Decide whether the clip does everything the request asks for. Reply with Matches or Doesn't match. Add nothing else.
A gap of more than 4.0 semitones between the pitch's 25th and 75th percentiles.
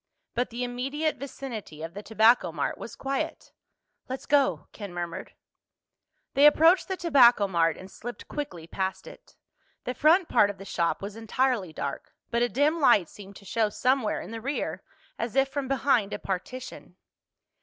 Matches